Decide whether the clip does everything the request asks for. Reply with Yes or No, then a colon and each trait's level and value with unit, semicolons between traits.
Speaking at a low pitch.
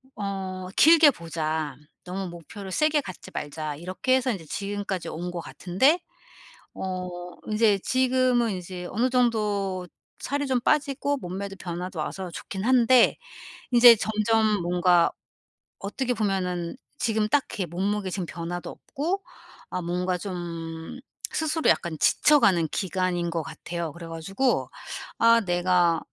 No: high, 190 Hz